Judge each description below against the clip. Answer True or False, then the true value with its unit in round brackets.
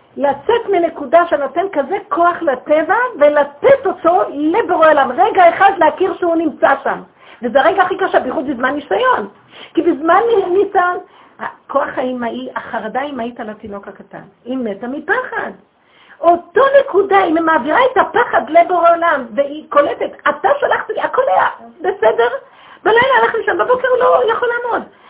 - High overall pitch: True (335 Hz)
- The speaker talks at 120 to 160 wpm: True (145 wpm)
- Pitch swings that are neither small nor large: False (5.9 semitones)